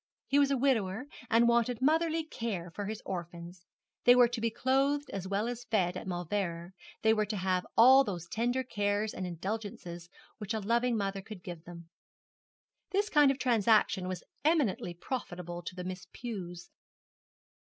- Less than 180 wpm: Yes, average, 170 wpm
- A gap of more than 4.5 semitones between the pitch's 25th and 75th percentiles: Yes, average, 5.2 semitones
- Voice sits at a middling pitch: No, high, 210 Hz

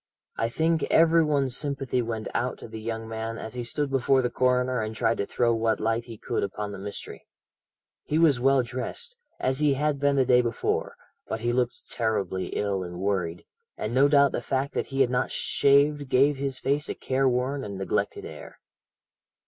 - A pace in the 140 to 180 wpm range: No, average, 195 wpm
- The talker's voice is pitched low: Yes, low, 125 Hz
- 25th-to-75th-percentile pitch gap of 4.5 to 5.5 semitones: No, average, 3.8 semitones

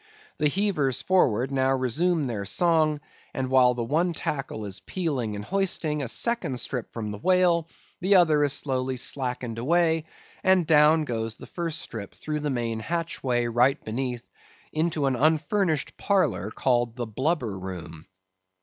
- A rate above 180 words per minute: No, average, 155 wpm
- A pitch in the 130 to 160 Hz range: Yes, low, 135 Hz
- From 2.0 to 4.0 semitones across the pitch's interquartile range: No, average, 5.3 semitones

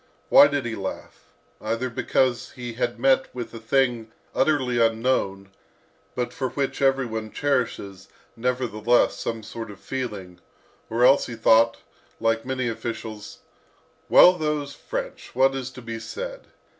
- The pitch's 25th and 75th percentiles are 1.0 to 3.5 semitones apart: Yes, average, 2.9 semitones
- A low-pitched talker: Yes, low, 120 Hz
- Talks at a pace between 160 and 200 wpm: No, average, 145 wpm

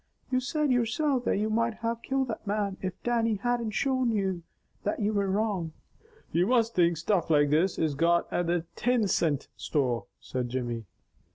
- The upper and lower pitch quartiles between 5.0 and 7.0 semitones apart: Yes, wide, 5.6 semitones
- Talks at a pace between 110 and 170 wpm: No, average, 180 wpm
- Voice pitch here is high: Yes, high, 205 Hz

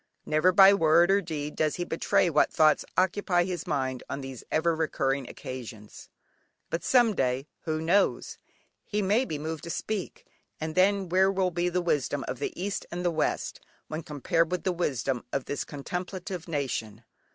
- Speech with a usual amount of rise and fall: Yes, average, 4.2 semitones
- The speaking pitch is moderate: Yes, medium, 165 Hz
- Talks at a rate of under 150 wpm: No, average, 175 wpm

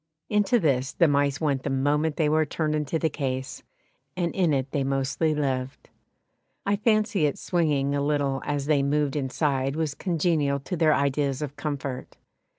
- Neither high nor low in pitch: Yes, medium, 145 Hz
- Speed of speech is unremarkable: Yes, average, 170 wpm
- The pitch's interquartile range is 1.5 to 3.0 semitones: Yes, narrow, 2.5 semitones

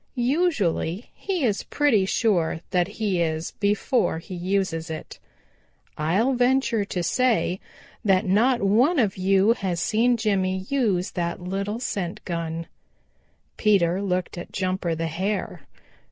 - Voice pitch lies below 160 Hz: No, high, 195 Hz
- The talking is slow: Yes, slow, 130 wpm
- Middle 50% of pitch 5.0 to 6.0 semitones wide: No, average, 4.5 semitones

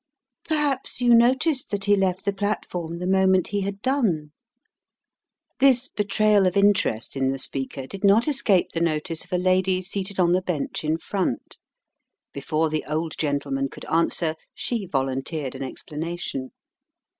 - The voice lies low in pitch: No, medium, 185 Hz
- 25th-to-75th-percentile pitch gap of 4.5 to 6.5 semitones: Yes, average, 4.9 semitones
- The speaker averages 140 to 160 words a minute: Yes, average, 155 wpm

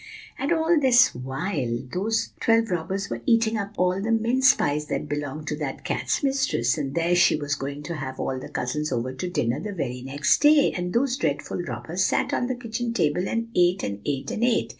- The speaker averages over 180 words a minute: Yes, fast, 205 wpm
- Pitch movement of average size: No, wide, 8.2 semitones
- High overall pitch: No, medium, 180 Hz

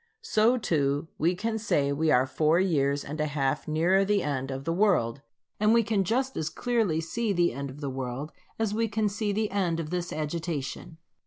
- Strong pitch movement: Yes, wide, 6.5 semitones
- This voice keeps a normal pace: No, fast, 210 wpm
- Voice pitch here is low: No, medium, 165 Hz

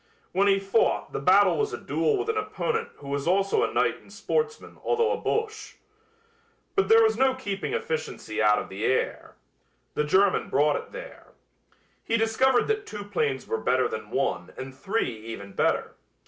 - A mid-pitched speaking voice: No, high, 200 Hz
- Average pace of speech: Yes, average, 180 wpm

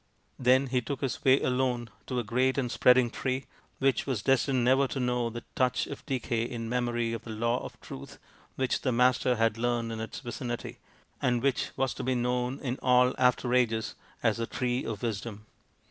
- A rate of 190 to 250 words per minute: Yes, average, 195 wpm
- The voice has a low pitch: Yes, low, 125 Hz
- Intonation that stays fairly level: Yes, narrow, 1.7 semitones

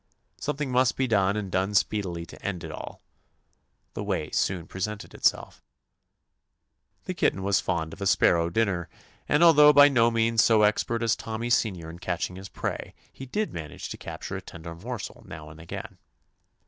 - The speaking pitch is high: No, low, 100 Hz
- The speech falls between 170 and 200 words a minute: Yes, average, 185 wpm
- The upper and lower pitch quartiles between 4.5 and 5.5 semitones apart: Yes, average, 5.1 semitones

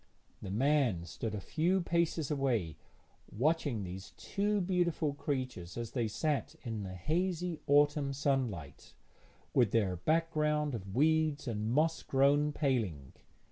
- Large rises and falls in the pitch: Yes, wide, 6.5 semitones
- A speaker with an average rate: No, slow, 130 wpm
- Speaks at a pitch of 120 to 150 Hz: Yes, medium, 140 Hz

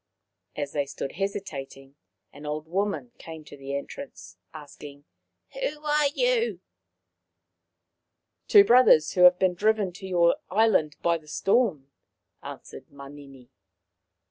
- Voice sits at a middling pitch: Yes, medium, 165 Hz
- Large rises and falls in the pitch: Yes, wide, 6.3 semitones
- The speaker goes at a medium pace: No, slow, 130 wpm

